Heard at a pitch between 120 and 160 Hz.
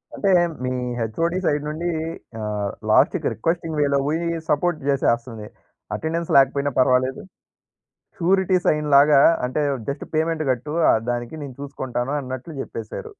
Yes: medium, 140 Hz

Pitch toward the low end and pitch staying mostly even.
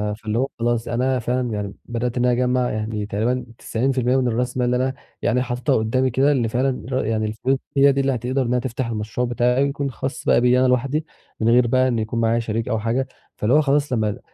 Yes: low, 125 Hz; narrow, 2.2 semitones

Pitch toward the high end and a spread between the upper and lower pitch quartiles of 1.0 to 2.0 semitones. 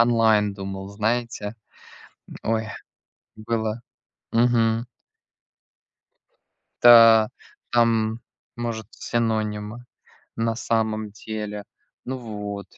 No: low, 110 Hz; narrow, 1.7 semitones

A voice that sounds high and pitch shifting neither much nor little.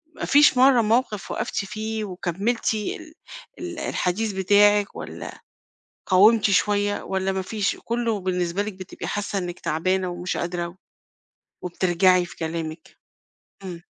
Yes: high, 195 Hz; average, 3.3 semitones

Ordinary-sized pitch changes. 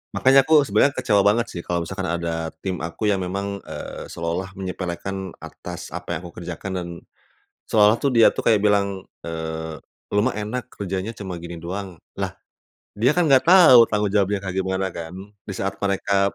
Yes: average, 3.1 semitones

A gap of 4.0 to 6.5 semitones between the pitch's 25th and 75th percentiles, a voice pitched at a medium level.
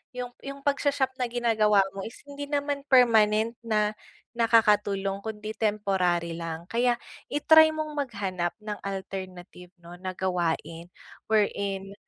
No: average, 4.4 semitones; high, 210 Hz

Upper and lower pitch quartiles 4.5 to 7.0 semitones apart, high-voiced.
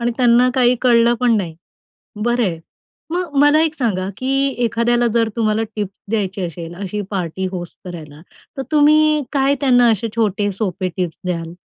Yes: average, 5.2 semitones; high, 230 Hz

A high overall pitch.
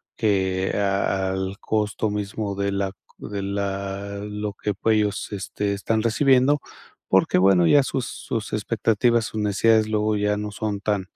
No: low, 105 Hz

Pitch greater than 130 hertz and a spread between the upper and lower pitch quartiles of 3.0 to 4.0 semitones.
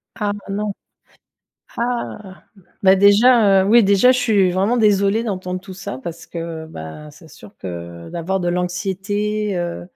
Yes: high, 190 Hz; average, 3.5 semitones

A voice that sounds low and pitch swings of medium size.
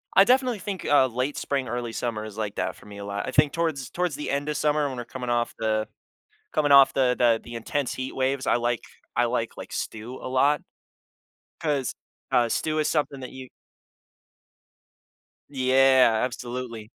Yes: low, 130 Hz; average, 3.4 semitones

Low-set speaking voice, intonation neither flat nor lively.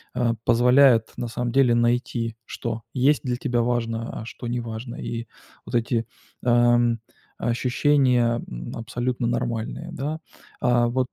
No: low, 120 Hz; narrow, 1.1 semitones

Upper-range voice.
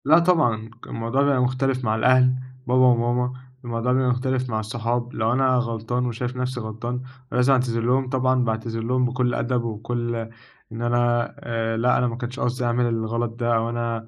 No: low, 120 Hz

